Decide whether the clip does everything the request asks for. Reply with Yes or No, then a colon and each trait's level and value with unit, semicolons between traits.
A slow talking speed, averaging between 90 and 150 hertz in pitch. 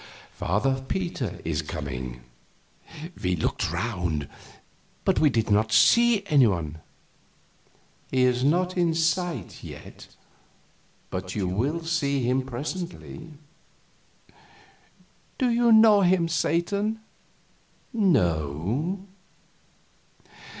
Yes: slow, 90 wpm; low, 135 Hz